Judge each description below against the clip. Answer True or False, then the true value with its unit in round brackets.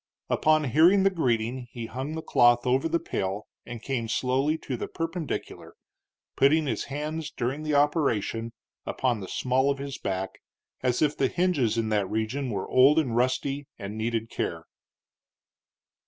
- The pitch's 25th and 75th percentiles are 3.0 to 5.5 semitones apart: True (4.7 semitones)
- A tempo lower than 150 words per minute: False (160 wpm)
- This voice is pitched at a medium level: False (130 Hz)